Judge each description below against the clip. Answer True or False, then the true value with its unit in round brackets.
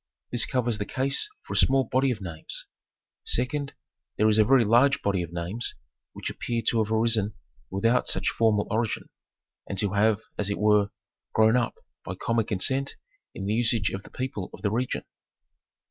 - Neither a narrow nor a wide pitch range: True (3.3 semitones)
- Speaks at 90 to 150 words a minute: False (180 wpm)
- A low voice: True (110 Hz)